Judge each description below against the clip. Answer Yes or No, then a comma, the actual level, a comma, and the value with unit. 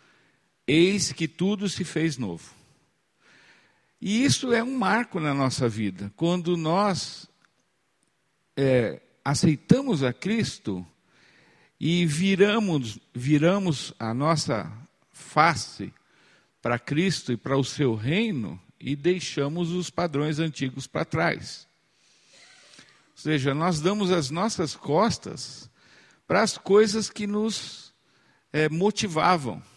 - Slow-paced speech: Yes, slow, 110 wpm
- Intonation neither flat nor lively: No, wide, 5.8 semitones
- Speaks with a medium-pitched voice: Yes, medium, 165 Hz